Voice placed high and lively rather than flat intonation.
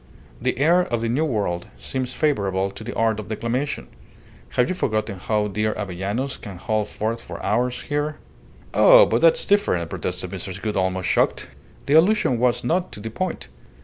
No: low, 115 Hz; wide, 6.2 semitones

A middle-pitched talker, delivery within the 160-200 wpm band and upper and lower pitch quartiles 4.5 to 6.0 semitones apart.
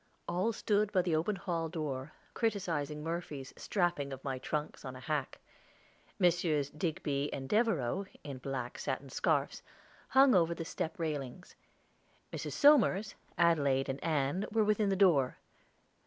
No: medium, 160 Hz; average, 140 wpm; average, 5.2 semitones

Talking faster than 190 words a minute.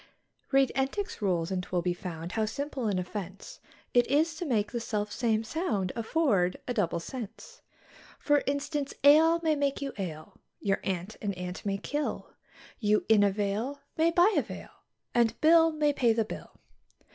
No: average, 175 wpm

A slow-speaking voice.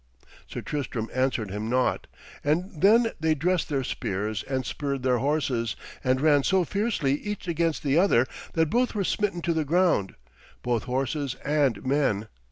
No: average, 165 wpm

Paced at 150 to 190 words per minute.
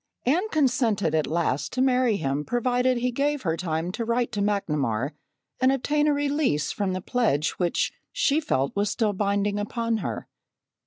Yes: average, 170 wpm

